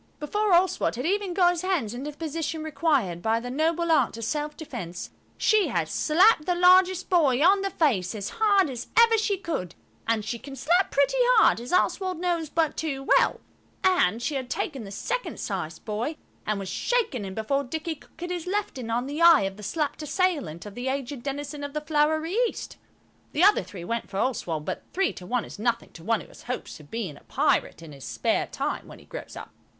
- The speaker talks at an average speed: No, fast, 215 wpm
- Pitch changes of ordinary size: No, wide, 7.4 semitones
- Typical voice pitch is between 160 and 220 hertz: No, very high, 290 Hz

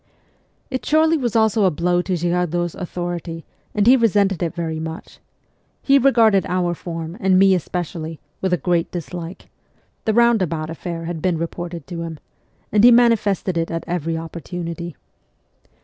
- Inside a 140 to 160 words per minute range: Yes, average, 150 wpm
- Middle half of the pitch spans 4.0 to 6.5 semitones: No, average, 3.3 semitones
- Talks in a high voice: No, medium, 175 Hz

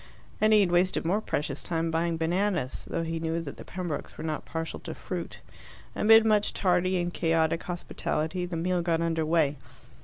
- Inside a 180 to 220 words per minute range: Yes, average, 185 wpm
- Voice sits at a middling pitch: Yes, medium, 170 Hz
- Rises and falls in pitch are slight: Yes, narrow, 2.0 semitones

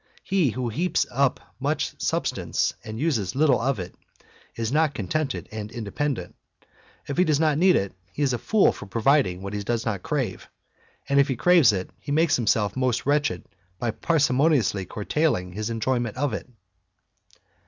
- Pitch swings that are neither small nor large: No, wide, 5.7 semitones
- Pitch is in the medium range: No, low, 125 Hz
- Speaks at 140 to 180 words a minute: Yes, average, 175 wpm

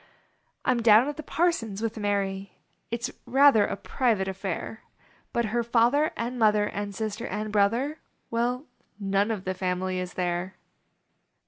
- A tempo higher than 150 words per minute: Yes, average, 160 wpm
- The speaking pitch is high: Yes, high, 215 Hz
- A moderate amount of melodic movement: Yes, average, 3.5 semitones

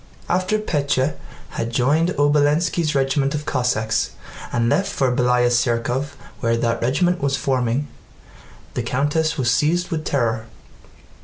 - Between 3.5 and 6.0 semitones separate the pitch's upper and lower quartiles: Yes, average, 3.9 semitones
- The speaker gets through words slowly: Yes, slow, 130 wpm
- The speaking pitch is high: No, low, 135 Hz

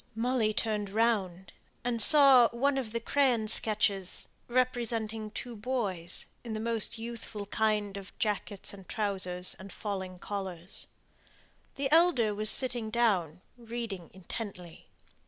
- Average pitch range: Yes, average, 3.3 semitones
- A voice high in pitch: Yes, high, 215 Hz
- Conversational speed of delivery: No, slow, 125 wpm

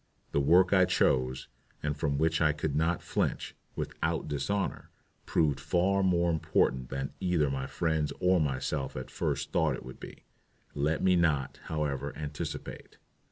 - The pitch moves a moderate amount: Yes, average, 3.8 semitones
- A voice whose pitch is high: No, very low, 75 Hz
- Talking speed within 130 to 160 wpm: Yes, average, 155 wpm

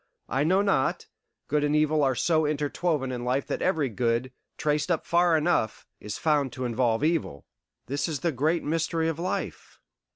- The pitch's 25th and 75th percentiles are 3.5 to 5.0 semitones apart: Yes, average, 3.8 semitones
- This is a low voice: No, medium, 150 Hz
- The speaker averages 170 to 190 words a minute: Yes, average, 175 wpm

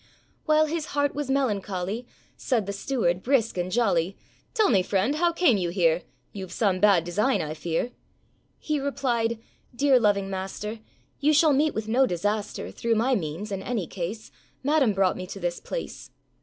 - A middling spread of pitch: No, wide, 6.2 semitones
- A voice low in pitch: No, high, 215 Hz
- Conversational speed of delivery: Yes, average, 170 wpm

